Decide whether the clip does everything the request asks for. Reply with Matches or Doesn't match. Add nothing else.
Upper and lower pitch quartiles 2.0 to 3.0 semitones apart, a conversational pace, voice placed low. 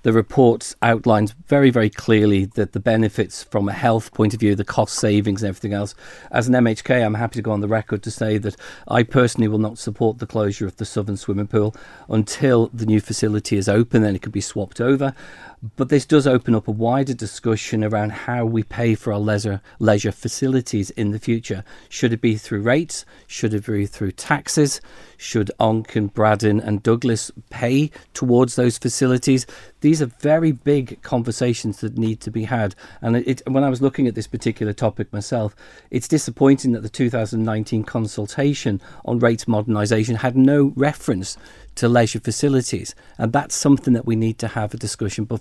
Matches